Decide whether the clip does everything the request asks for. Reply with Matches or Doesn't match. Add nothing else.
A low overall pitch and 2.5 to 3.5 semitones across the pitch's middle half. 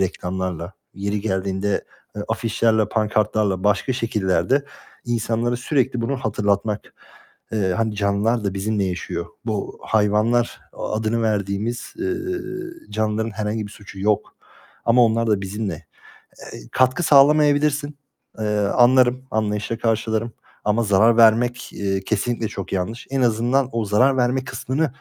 Matches